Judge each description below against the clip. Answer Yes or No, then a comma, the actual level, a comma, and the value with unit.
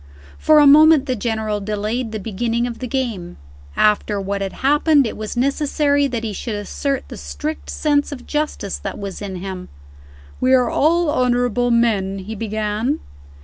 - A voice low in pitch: No, high, 235 Hz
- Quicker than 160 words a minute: Yes, average, 170 wpm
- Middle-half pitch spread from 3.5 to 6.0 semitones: Yes, average, 5.1 semitones